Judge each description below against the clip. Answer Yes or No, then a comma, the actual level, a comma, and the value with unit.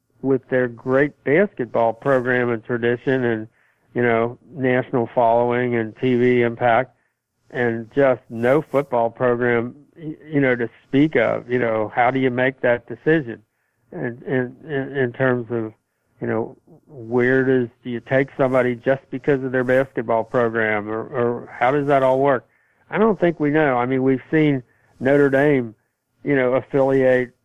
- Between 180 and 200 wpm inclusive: No, average, 165 wpm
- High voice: No, low, 125 Hz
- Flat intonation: Yes, narrow, 2.2 semitones